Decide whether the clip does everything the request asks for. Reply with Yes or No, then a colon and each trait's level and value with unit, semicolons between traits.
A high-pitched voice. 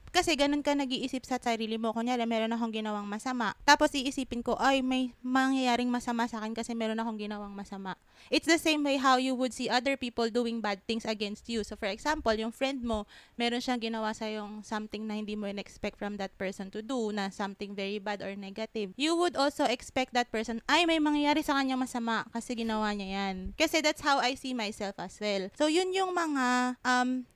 Yes: high, 235 Hz